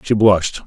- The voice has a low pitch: Yes, low, 100 Hz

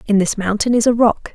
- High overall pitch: Yes, high, 215 Hz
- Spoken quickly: Yes, fast, 265 wpm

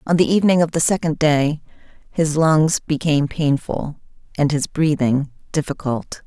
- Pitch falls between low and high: Yes, medium, 150 Hz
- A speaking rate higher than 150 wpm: No, average, 145 wpm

